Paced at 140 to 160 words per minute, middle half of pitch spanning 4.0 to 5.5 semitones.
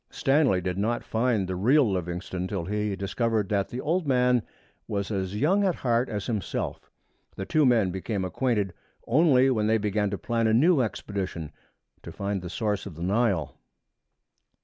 No: average, 170 wpm; average, 4.5 semitones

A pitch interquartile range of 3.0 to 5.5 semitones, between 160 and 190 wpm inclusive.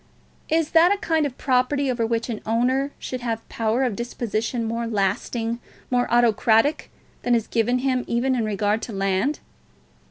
No: narrow, 2.5 semitones; average, 170 wpm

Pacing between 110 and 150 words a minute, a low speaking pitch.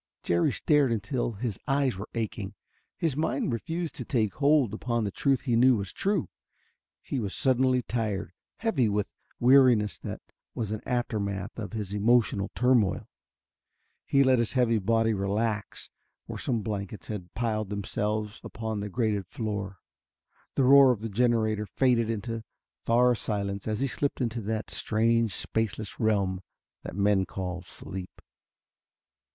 Yes: average, 145 wpm; low, 110 Hz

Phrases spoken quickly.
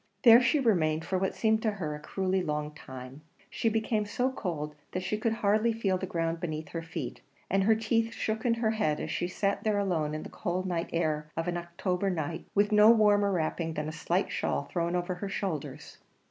Yes: fast, 215 wpm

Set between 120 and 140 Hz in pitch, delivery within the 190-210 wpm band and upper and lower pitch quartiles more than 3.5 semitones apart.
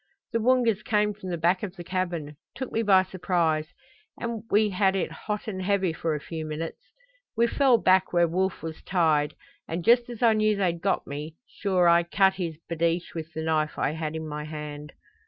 No: medium, 180 Hz; fast, 205 wpm; average, 4.6 semitones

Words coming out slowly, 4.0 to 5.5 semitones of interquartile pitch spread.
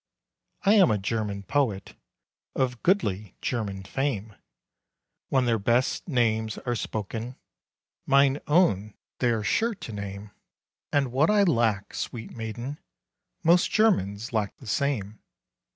Yes: slow, 125 wpm; average, 5.1 semitones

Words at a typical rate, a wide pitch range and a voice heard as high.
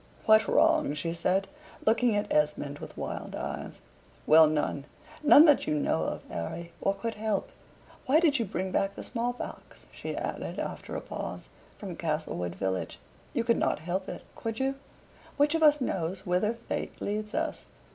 Yes: average, 175 wpm; wide, 6.7 semitones; high, 195 Hz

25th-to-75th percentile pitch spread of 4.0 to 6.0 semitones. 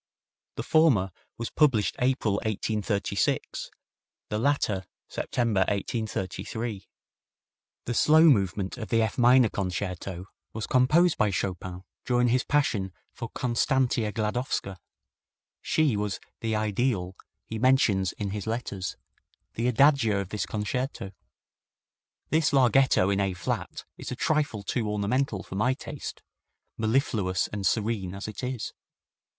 Yes: average, 4.3 semitones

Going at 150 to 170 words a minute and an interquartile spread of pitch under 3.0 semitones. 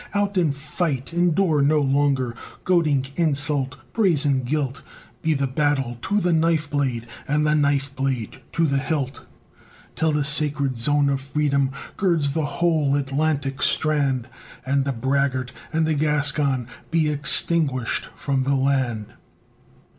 No: average, 140 wpm; narrow, 2.4 semitones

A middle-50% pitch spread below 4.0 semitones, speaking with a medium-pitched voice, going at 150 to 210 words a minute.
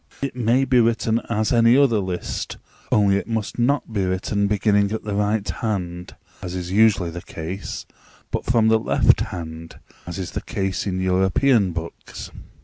No: average, 3.6 semitones; low, 100 Hz; average, 170 wpm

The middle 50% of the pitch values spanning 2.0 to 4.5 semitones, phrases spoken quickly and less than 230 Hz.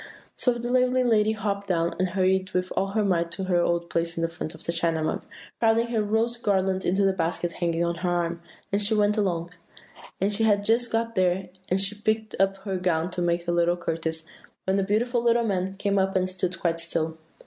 Yes: average, 3.6 semitones; fast, 225 wpm; high, 190 Hz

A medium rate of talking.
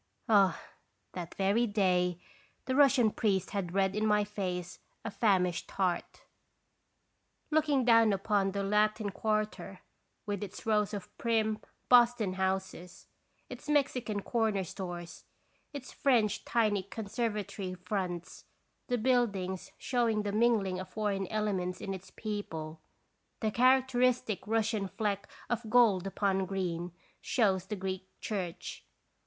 No: slow, 125 wpm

